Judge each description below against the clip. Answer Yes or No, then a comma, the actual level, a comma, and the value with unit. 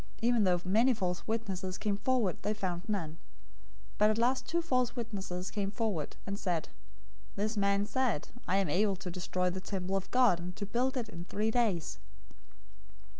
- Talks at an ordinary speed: Yes, average, 180 wpm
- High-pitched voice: Yes, high, 200 Hz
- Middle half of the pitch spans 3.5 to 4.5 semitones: Yes, average, 3.9 semitones